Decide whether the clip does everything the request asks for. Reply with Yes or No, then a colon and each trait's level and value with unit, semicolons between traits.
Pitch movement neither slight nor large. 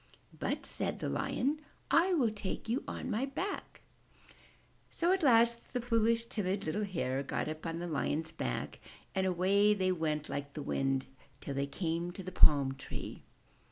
No: wide, 7.0 semitones